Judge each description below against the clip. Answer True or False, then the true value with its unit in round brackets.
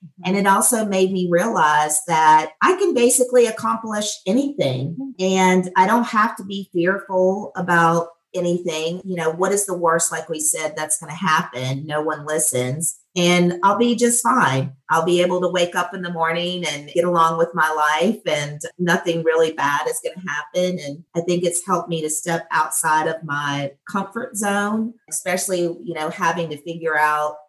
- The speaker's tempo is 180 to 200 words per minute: True (185 wpm)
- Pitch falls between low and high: True (170 Hz)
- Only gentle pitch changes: False (3.3 semitones)